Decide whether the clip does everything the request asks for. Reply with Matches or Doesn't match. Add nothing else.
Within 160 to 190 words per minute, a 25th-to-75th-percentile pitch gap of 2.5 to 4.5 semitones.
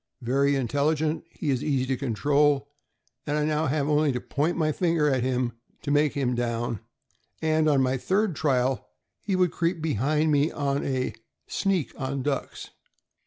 Matches